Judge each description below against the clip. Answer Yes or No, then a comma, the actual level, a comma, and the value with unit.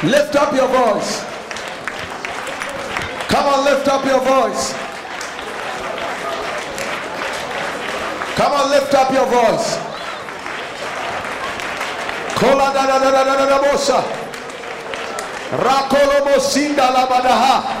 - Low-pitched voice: No, very high, 275 Hz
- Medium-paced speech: No, slow, 90 wpm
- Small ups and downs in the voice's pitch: Yes, narrow, 1.1 semitones